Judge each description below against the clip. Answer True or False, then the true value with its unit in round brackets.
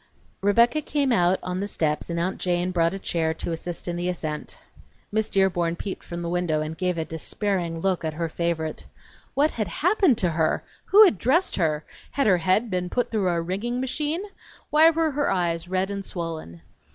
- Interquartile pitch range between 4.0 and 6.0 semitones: True (4.8 semitones)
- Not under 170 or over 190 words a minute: False (200 wpm)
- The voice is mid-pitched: True (180 Hz)